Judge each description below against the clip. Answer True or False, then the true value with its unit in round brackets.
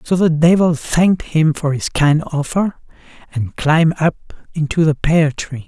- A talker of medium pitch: True (160 Hz)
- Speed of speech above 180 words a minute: False (170 wpm)